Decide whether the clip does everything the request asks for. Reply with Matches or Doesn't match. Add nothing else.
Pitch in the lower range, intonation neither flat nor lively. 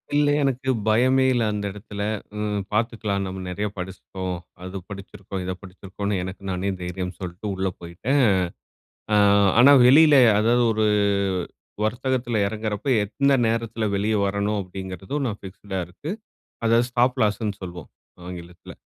Matches